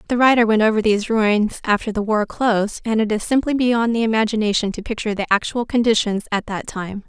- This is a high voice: Yes, high, 220 Hz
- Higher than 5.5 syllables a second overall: Yes, 6.0 syllables/s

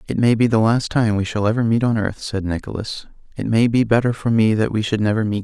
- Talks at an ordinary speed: No, fast, 285 wpm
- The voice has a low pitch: Yes, low, 110 Hz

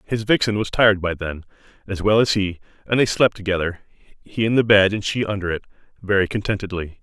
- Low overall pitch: Yes, low, 100 Hz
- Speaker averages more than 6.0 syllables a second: Yes, 6.2 syllables/s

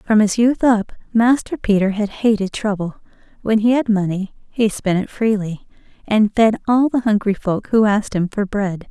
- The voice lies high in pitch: Yes, high, 210 Hz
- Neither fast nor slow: Yes, average, 190 wpm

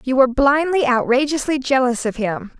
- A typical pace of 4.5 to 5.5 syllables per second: Yes, 5.3 syllables/s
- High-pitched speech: Yes, very high, 260 Hz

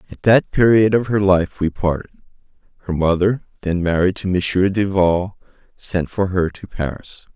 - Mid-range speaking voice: No, very low, 95 Hz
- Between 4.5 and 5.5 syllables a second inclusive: Yes, 4.7 syllables/s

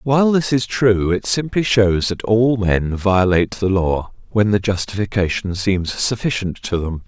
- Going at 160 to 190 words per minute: Yes, average, 170 wpm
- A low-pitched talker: Yes, low, 105 Hz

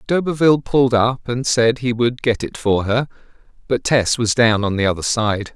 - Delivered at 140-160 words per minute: No, fast, 205 wpm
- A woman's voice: No, male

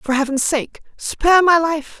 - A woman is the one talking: Yes, female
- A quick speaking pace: No, average, 180 wpm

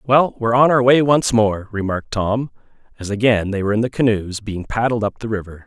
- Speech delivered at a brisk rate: Yes, fast, 220 wpm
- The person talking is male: Yes, male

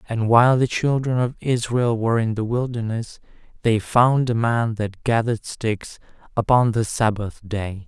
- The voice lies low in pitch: Yes, low, 115 Hz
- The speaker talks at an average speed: Yes, average, 160 wpm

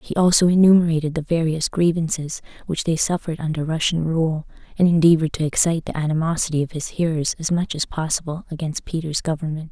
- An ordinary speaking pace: Yes, average, 175 wpm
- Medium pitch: Yes, medium, 160 Hz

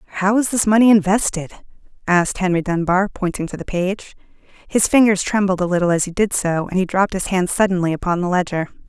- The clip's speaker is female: Yes, female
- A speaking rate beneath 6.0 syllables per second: No, 6.2 syllables/s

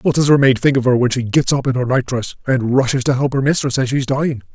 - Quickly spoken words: Yes, fast, 305 wpm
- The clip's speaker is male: Yes, male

